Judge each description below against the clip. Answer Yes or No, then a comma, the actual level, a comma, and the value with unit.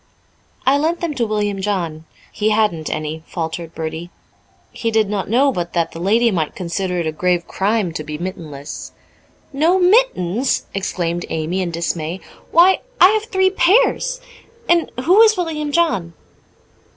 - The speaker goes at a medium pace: Yes, average, 155 wpm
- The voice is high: Yes, high, 195 Hz